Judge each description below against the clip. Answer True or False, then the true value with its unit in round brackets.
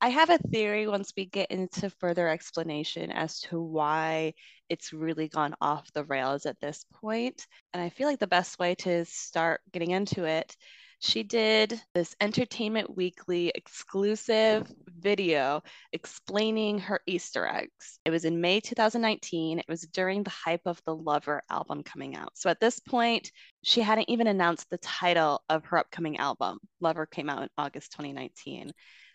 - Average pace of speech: True (165 wpm)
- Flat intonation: False (4.6 semitones)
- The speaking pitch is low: False (175 Hz)